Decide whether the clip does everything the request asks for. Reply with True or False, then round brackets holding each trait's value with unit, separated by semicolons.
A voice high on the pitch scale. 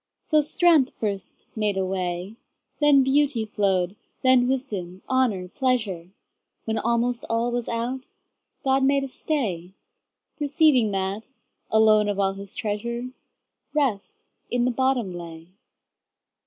True (230 Hz)